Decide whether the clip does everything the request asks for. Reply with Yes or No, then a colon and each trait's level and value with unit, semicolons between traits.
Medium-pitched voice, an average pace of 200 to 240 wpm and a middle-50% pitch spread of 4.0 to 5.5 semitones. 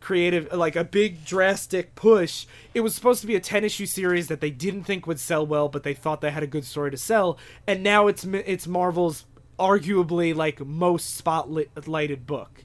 Yes: medium, 175 Hz; fast, 205 wpm; average, 4.5 semitones